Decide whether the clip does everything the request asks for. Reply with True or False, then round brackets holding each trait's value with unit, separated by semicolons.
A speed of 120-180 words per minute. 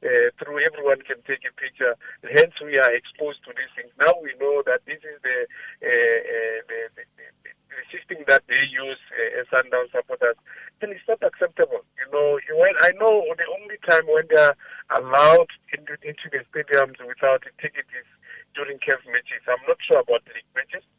False (190 wpm)